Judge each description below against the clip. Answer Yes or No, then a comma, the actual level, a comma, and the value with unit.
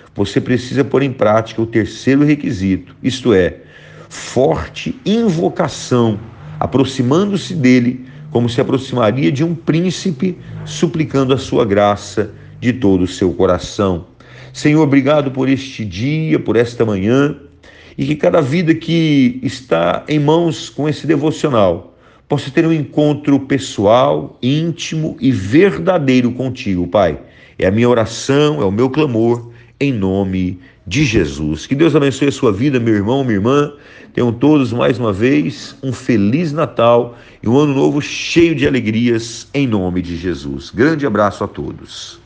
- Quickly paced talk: No, average, 145 wpm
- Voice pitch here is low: Yes, low, 130 Hz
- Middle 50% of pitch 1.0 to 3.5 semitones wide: No, average, 4.8 semitones